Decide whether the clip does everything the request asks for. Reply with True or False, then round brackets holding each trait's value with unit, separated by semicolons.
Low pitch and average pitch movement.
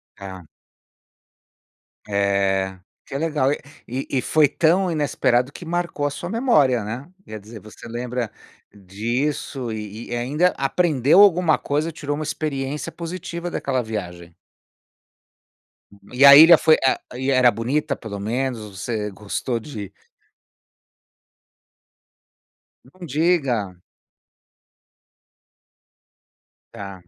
False (130 Hz; 6.1 semitones)